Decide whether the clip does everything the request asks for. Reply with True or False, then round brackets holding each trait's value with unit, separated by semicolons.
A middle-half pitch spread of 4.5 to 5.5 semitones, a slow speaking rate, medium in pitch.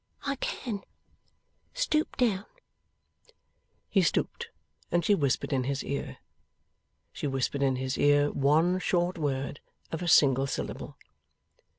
True (5.2 semitones; 120 wpm; 150 Hz)